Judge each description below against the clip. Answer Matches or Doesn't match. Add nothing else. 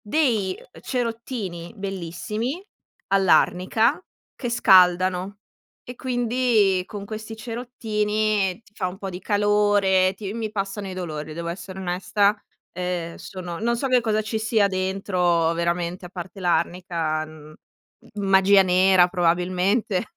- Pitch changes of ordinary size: Matches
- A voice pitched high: Matches